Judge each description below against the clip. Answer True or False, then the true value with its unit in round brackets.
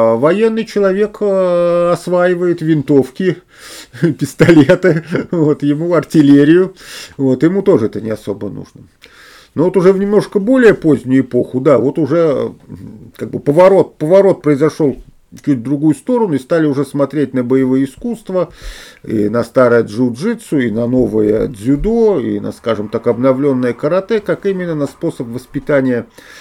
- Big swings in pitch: True (5.7 semitones)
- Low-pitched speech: False (150 Hz)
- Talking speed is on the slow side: False (135 wpm)